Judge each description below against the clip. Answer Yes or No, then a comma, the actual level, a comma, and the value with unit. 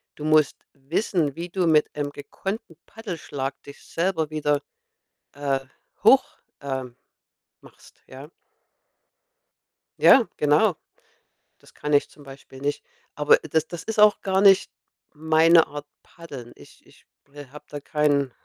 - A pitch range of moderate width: Yes, average, 3.0 semitones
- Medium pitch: Yes, medium, 150 Hz